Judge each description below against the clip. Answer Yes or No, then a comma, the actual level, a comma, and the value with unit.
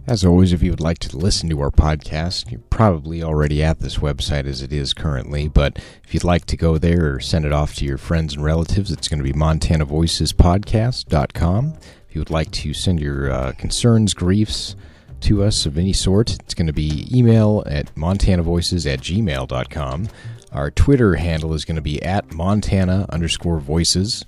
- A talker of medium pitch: No, very low, 80 Hz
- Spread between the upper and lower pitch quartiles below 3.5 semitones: No, average, 4.2 semitones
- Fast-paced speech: No, average, 190 wpm